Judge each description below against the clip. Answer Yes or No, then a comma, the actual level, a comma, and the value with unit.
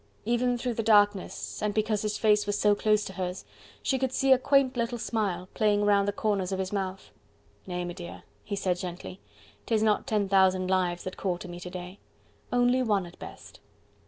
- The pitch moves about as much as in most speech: Yes, average, 3.0 semitones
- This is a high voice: Yes, high, 205 Hz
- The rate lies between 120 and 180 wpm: No, average, 200 wpm